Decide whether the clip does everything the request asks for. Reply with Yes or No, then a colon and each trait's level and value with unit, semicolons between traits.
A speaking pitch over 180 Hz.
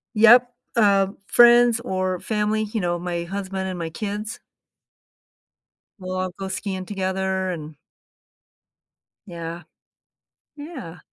Yes: high, 190 Hz